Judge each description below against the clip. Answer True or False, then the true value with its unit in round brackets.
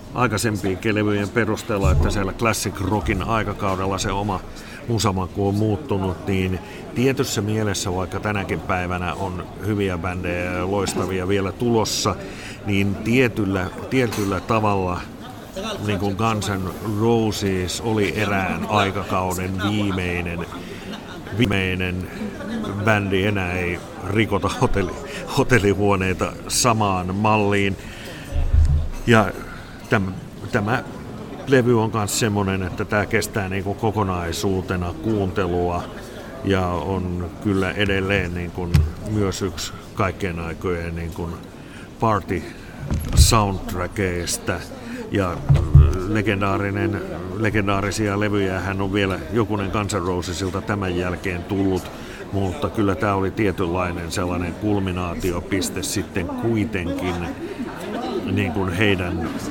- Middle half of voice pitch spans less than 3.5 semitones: True (2.6 semitones)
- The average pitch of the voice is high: False (100 Hz)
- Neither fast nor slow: False (90 wpm)